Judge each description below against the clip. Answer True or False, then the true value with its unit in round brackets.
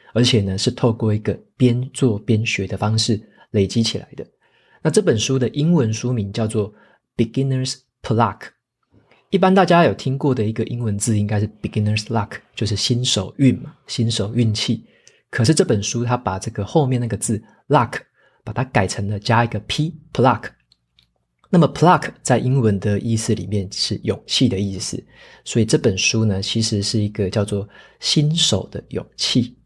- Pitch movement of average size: True (3.5 semitones)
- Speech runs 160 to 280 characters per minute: False (315 characters per minute)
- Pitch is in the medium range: False (115 Hz)